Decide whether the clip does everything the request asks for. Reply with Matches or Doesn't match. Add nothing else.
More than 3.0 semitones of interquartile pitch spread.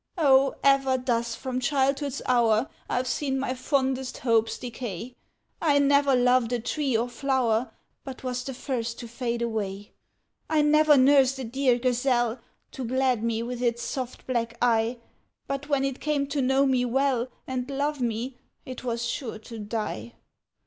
Doesn't match